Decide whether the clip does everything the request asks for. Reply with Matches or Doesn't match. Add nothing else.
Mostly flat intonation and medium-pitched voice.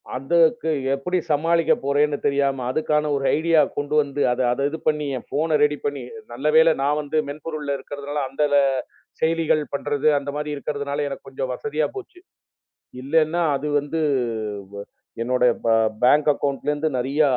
Matches